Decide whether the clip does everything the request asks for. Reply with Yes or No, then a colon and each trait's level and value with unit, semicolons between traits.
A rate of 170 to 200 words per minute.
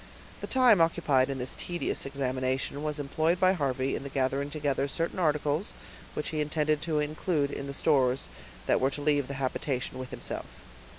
Yes: average, 175 wpm